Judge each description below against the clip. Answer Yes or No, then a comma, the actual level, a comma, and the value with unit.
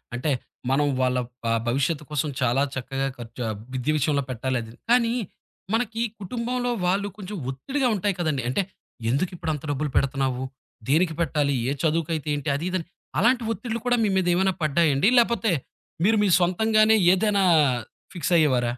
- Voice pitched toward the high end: No, medium, 160 Hz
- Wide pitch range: Yes, wide, 7.2 semitones